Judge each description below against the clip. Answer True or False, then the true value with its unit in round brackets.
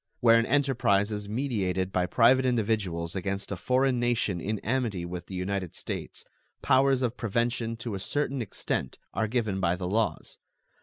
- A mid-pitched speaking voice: False (110 Hz)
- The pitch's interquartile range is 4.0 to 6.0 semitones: True (4.4 semitones)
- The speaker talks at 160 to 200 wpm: True (165 wpm)